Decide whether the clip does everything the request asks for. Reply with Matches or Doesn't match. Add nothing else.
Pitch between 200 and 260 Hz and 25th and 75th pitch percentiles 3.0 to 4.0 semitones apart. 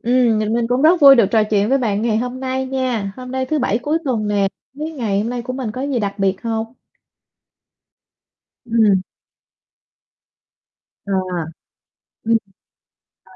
Matches